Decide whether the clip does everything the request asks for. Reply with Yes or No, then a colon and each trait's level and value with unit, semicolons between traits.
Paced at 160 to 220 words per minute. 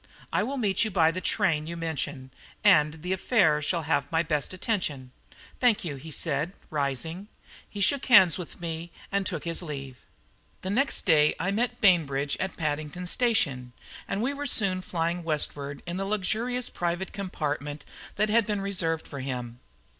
Yes: average, 170 wpm